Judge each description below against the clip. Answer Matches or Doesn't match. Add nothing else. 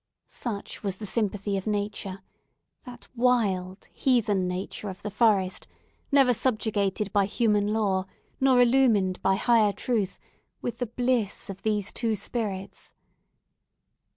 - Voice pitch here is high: Matches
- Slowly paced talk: Matches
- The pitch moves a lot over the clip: Doesn't match